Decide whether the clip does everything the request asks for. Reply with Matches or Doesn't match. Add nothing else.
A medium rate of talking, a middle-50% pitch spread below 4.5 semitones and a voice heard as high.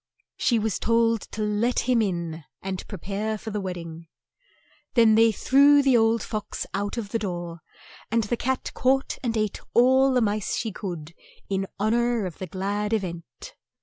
Matches